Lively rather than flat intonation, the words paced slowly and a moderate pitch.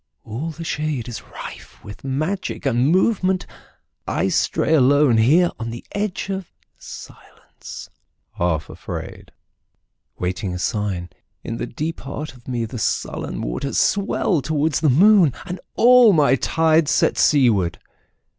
Yes: wide, 6.5 semitones; slow, 120 wpm; medium, 145 Hz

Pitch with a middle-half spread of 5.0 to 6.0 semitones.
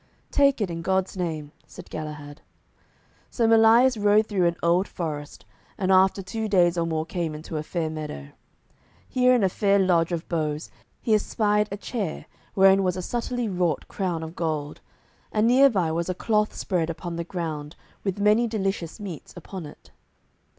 No: average, 4.3 semitones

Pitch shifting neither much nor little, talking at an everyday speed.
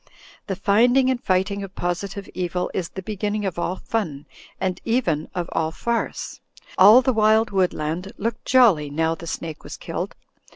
Yes: average, 4.3 semitones; average, 175 wpm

